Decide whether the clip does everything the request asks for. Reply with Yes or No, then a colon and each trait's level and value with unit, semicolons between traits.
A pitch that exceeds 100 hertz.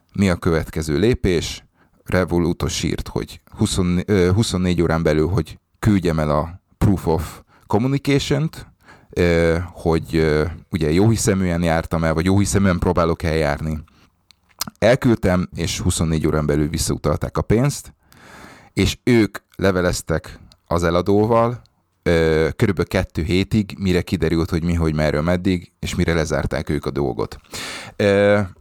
No: very low, 90 Hz